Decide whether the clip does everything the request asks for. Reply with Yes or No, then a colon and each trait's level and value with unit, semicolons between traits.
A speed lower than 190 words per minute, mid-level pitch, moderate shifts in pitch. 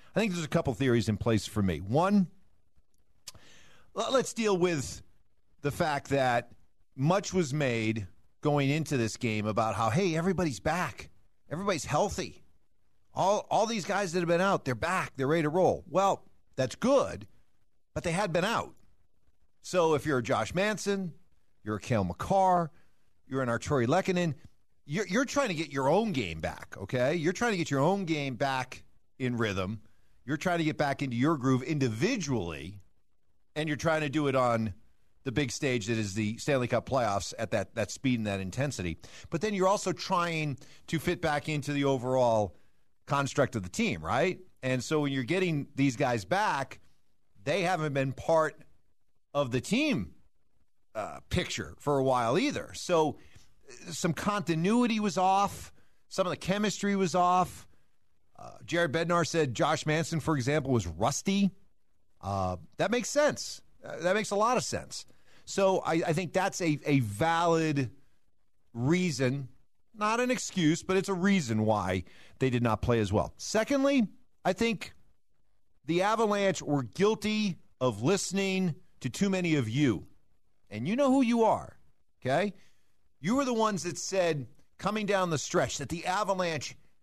No: average, 170 wpm; medium, 145 Hz; wide, 8.3 semitones